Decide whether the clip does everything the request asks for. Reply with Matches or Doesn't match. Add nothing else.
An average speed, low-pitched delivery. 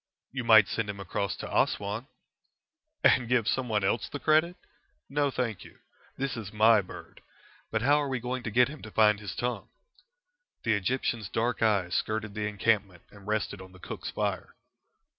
Matches